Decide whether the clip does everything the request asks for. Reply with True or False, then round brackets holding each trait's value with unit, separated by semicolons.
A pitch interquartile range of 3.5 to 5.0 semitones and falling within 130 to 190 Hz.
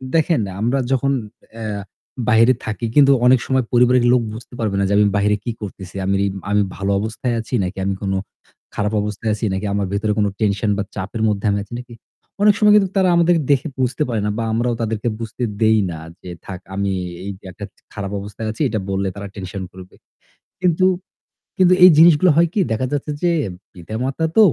False (4.5 semitones; 110 Hz)